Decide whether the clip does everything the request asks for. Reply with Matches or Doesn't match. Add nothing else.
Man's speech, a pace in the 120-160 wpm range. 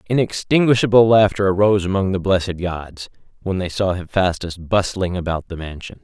Matches